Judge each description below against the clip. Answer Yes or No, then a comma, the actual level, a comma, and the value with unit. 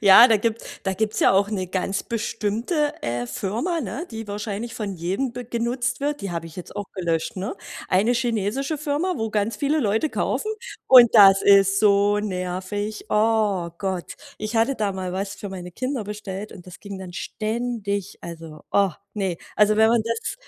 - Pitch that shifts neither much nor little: Yes, average, 3.3 semitones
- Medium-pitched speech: No, high, 210 Hz